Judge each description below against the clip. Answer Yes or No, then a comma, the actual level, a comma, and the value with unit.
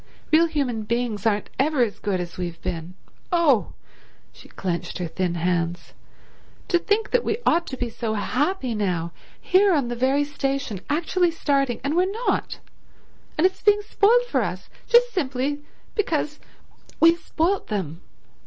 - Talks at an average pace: Yes, average, 150 wpm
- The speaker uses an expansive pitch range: Yes, wide, 8.9 semitones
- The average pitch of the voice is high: Yes, very high, 275 Hz